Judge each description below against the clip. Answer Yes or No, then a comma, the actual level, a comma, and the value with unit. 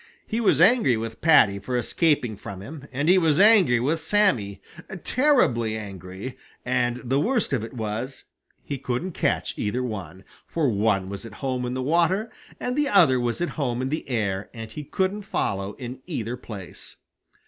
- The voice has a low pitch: Yes, low, 125 Hz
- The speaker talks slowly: No, average, 180 wpm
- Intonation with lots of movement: Yes, wide, 7.1 semitones